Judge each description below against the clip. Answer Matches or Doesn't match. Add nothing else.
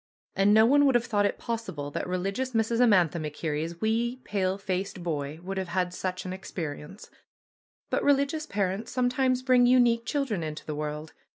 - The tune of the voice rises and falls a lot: Matches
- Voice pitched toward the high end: Matches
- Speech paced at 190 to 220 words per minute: Doesn't match